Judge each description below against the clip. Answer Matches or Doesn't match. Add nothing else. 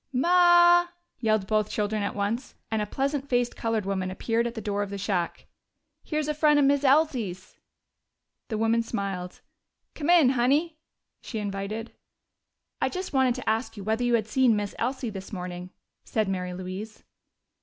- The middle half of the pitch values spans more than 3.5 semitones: Matches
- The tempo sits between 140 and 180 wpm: Matches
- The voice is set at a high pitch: Matches